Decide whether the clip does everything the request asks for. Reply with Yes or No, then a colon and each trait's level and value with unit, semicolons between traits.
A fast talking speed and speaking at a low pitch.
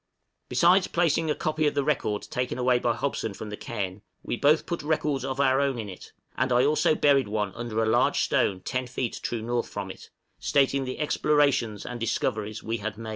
Yes: fast, 210 wpm; low, 125 Hz